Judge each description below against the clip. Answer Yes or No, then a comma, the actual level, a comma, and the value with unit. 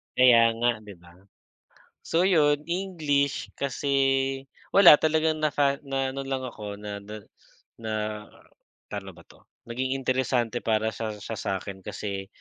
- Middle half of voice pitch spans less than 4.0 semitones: No, average, 4.6 semitones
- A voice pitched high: No, low, 130 Hz